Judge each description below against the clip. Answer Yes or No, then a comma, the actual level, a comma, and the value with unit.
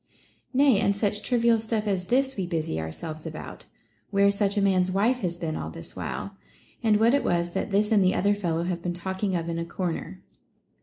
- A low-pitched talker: No, high, 195 Hz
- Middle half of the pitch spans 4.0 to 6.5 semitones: No, average, 3.5 semitones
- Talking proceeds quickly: Yes, fast, 220 wpm